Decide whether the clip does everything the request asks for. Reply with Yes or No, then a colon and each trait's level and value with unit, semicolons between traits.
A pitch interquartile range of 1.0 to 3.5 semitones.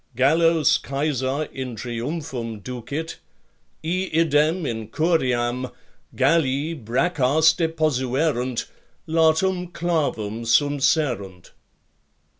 No: average, 4.7 semitones